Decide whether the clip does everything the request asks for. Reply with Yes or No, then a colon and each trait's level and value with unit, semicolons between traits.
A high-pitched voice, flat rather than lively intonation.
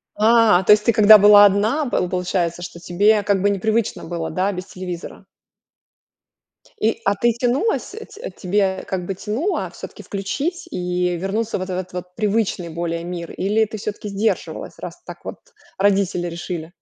No: high, 200 Hz; average, 3.3 semitones